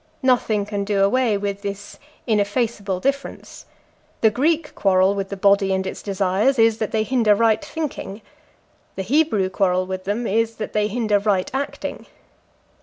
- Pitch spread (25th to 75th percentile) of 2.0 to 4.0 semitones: Yes, average, 2.8 semitones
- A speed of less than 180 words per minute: Yes, average, 160 wpm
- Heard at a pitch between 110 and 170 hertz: No, high, 210 Hz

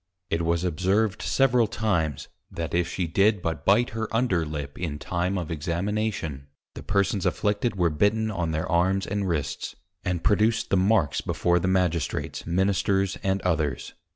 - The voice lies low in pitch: Yes, very low, 90 Hz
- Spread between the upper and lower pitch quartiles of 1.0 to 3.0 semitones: No, average, 3.6 semitones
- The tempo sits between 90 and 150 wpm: No, average, 160 wpm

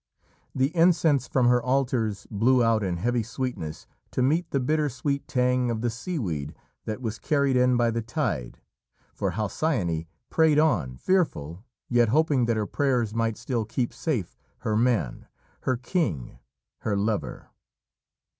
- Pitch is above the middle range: No, low, 120 Hz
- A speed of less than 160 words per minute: Yes, average, 150 wpm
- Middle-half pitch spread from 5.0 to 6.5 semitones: No, average, 4.2 semitones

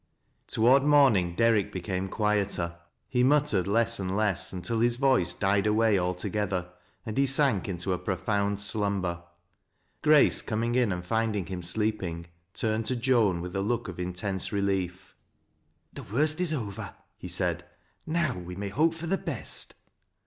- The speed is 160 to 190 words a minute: Yes, average, 165 wpm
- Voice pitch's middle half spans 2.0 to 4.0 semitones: No, average, 4.4 semitones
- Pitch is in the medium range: No, low, 105 Hz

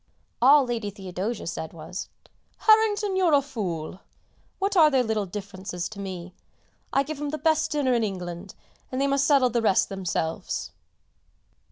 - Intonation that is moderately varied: No, wide, 7.5 semitones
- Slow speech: No, average, 160 wpm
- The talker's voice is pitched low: No, high, 230 Hz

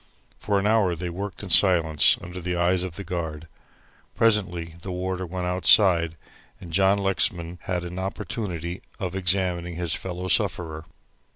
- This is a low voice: Yes, very low, 90 Hz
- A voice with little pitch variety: Yes, narrow, 1.9 semitones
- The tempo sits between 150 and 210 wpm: Yes, average, 155 wpm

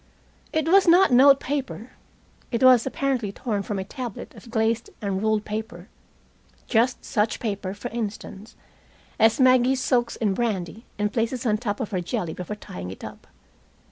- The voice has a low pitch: No, high, 225 Hz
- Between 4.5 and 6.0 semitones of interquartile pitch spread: No, average, 3.7 semitones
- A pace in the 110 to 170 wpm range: Yes, average, 165 wpm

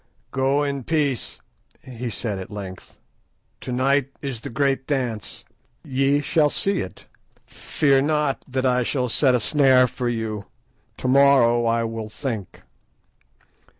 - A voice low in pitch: Yes, low, 130 Hz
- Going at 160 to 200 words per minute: No, average, 140 wpm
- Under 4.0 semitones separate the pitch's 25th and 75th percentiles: Yes, average, 3.2 semitones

